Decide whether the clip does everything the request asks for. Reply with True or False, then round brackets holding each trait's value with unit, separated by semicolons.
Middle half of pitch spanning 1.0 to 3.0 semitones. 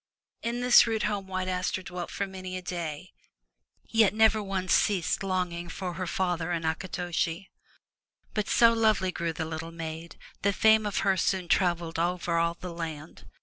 True (2.7 semitones)